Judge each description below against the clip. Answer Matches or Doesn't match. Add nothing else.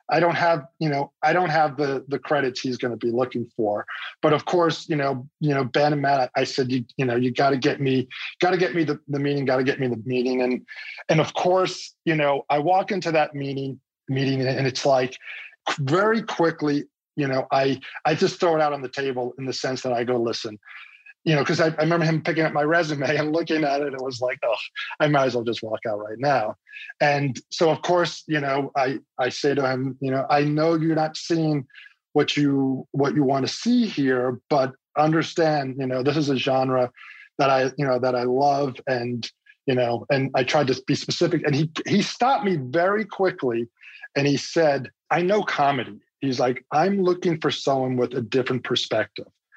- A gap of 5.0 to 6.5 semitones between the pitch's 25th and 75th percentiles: Doesn't match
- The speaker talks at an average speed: Doesn't match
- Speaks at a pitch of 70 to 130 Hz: Doesn't match